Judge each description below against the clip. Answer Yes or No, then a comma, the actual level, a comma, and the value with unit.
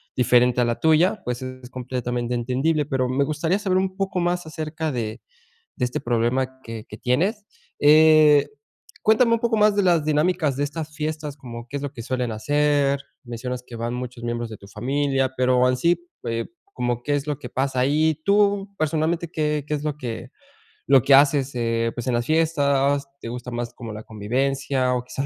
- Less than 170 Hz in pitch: Yes, low, 135 Hz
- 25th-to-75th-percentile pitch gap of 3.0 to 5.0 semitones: Yes, average, 4.1 semitones